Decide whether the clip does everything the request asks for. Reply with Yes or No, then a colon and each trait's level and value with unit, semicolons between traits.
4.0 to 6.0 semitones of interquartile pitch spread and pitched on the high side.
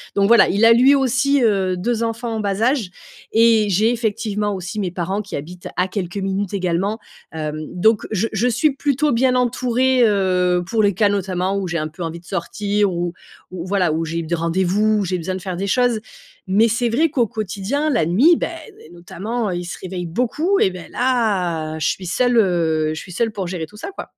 Yes: average, 4.5 semitones; high, 200 Hz